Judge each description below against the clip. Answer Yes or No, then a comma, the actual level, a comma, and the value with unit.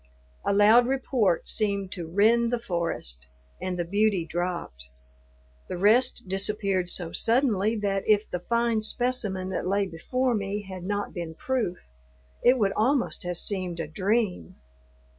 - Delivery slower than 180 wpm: Yes, average, 145 wpm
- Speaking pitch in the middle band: No, high, 200 Hz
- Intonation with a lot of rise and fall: No, average, 4.3 semitones